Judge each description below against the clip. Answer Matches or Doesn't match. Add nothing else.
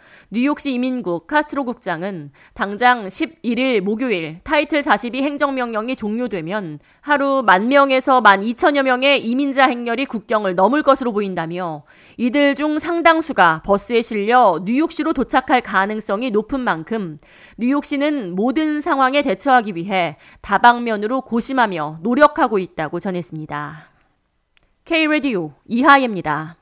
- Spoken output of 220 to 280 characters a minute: Doesn't match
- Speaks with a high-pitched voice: Matches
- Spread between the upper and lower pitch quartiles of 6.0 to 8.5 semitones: Matches